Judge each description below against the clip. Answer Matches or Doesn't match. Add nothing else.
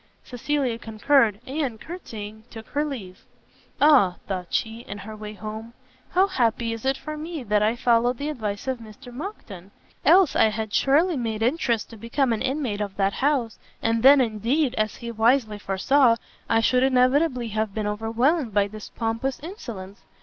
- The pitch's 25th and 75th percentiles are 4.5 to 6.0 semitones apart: Doesn't match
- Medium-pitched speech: Doesn't match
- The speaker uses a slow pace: Doesn't match